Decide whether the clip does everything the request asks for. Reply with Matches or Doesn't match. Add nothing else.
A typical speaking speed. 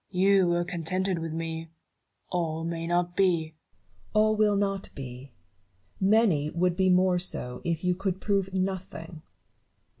Matches